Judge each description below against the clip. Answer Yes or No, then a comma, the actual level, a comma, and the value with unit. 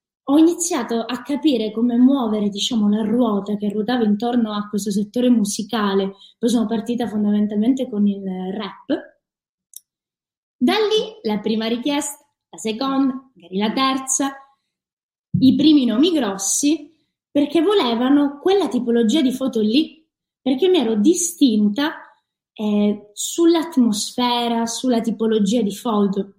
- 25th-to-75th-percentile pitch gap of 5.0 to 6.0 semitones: Yes, average, 5.3 semitones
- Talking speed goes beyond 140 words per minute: No, average, 125 wpm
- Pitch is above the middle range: Yes, high, 240 Hz